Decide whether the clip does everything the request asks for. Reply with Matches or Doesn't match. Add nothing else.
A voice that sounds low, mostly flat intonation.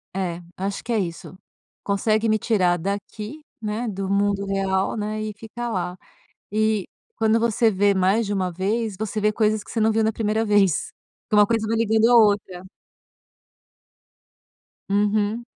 Doesn't match